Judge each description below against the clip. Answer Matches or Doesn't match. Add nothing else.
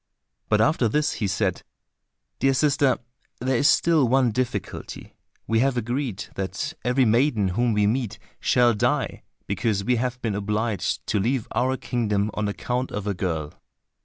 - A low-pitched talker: Matches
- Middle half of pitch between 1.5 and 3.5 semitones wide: Doesn't match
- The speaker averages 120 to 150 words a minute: Doesn't match